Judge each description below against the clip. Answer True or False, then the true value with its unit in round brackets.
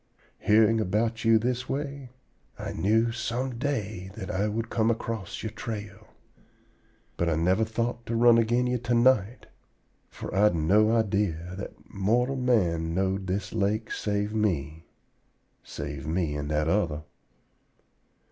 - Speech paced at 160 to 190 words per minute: False (140 wpm)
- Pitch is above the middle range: False (105 Hz)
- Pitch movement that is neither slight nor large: True (3.7 semitones)